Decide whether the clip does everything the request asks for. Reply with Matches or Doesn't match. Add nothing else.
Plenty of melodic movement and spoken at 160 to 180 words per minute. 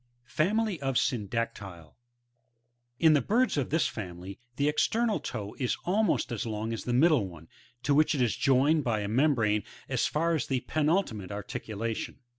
Matches